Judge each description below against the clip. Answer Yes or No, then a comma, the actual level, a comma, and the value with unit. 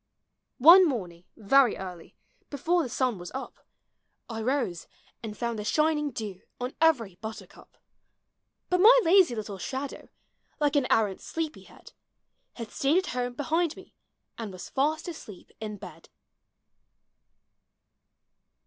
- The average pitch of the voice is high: Yes, very high, 250 Hz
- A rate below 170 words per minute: Yes, slow, 135 wpm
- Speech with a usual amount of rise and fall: No, wide, 6.4 semitones